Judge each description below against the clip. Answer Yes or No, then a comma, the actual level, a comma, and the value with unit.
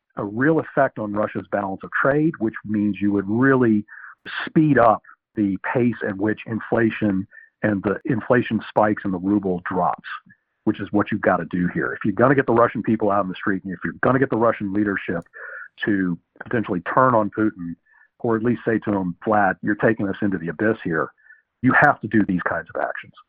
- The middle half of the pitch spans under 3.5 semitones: Yes, narrow, 2.5 semitones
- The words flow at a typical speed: No, fast, 210 wpm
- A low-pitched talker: Yes, low, 105 Hz